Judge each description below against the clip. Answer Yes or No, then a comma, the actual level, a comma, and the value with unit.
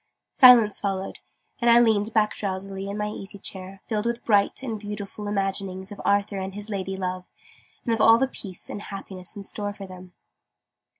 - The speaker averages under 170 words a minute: No, average, 185 wpm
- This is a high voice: Yes, high, 200 Hz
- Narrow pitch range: Yes, narrow, 1.9 semitones